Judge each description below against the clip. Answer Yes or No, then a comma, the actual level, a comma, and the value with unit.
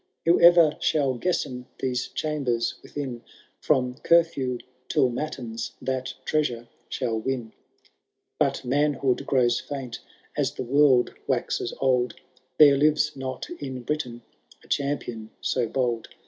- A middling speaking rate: No, slow, 120 wpm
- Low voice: Yes, low, 130 Hz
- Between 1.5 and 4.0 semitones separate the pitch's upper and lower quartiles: Yes, average, 3.1 semitones